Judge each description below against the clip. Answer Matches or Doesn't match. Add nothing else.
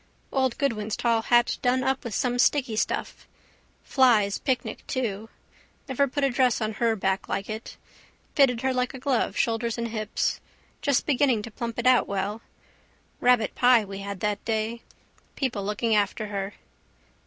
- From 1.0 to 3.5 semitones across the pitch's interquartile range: Matches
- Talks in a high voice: Matches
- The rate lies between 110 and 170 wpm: Matches